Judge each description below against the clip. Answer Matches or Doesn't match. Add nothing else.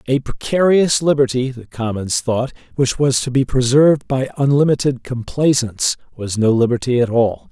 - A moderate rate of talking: Matches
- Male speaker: Matches